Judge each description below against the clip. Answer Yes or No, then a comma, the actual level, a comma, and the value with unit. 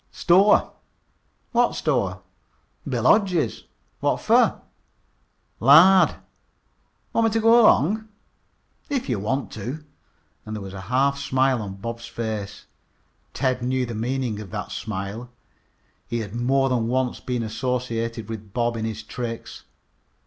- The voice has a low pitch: Yes, low, 125 Hz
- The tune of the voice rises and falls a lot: No, average, 3.7 semitones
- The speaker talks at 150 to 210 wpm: No, slow, 135 wpm